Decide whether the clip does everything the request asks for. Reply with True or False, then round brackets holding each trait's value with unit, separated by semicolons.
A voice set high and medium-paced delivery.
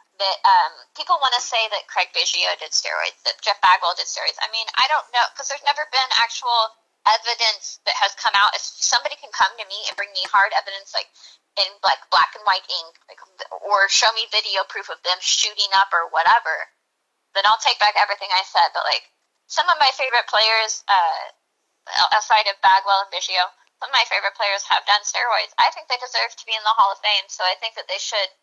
False (215 Hz; 225 wpm)